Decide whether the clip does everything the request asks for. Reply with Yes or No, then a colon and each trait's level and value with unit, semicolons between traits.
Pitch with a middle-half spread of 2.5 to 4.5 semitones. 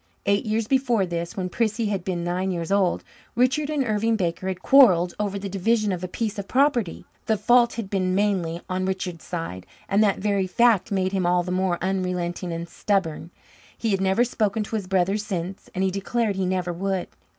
Yes: average, 3.0 semitones